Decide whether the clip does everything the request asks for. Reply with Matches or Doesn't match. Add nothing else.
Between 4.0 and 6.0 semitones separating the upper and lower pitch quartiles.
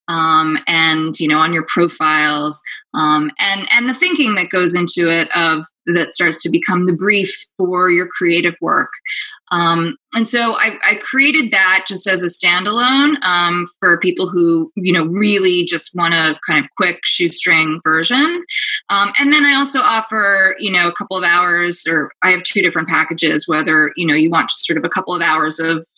Matches